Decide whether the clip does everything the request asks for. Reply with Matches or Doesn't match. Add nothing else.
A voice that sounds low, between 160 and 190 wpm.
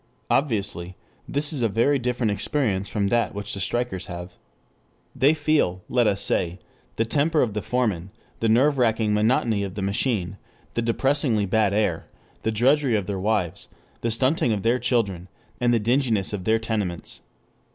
Matches